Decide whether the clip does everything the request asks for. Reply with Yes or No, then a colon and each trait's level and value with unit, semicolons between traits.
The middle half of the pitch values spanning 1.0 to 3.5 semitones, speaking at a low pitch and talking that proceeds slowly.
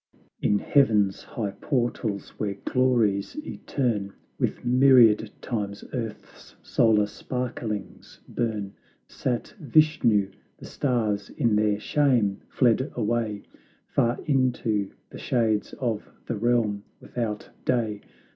Yes: average, 3.2 semitones; low, 115 Hz; slow, 105 wpm